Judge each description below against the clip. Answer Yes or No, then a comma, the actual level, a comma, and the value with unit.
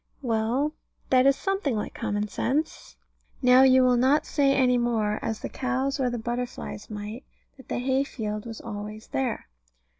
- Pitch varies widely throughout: No, average, 3.3 semitones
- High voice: Yes, very high, 250 Hz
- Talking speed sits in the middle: Yes, average, 170 wpm